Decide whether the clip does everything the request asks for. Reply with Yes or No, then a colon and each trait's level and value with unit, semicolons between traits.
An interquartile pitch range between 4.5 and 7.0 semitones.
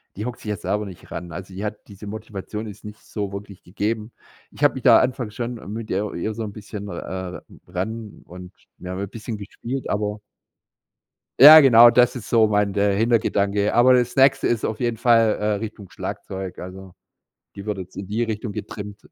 No: narrow, 2.5 semitones